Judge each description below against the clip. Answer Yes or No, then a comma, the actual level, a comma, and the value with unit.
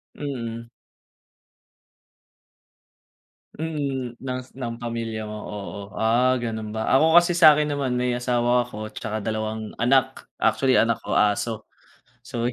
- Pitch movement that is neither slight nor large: Yes, average, 3.0 semitones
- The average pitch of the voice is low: Yes, low, 120 Hz